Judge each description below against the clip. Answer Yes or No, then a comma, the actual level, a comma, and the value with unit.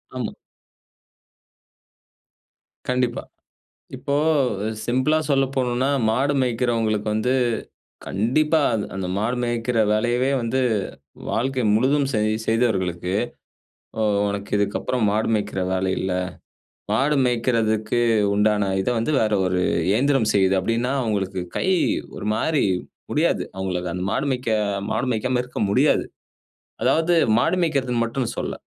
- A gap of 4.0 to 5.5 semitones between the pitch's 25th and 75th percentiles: No, average, 3.6 semitones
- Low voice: Yes, low, 115 Hz